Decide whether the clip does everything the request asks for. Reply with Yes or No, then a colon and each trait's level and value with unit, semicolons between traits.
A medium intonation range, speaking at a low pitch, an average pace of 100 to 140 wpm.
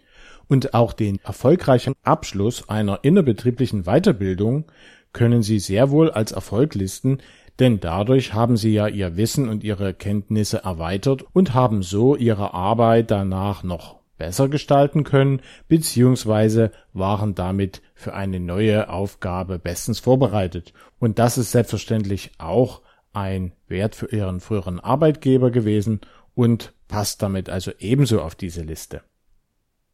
Yes: average, 4.6 semitones; low, 110 Hz; average, 130 wpm